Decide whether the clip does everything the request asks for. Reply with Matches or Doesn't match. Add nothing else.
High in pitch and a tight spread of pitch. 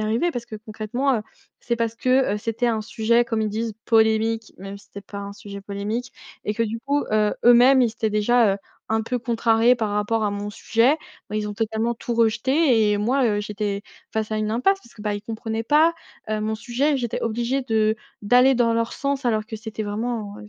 Matches